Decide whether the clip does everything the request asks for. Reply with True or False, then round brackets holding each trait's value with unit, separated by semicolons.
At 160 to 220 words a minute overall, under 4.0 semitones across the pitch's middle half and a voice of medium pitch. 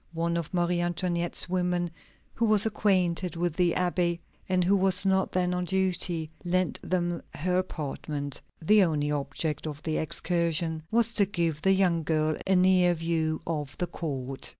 True (165 wpm; 2.4 semitones; 175 Hz)